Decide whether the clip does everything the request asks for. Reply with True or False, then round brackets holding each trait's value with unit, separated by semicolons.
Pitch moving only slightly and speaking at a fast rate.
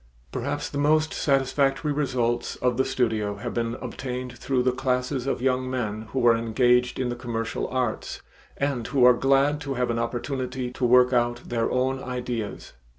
False (1.8 semitones; 175 wpm)